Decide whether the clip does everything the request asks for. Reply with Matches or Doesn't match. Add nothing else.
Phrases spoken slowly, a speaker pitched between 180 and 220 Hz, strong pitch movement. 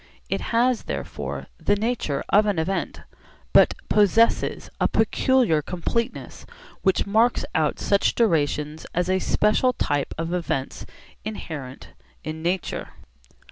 Matches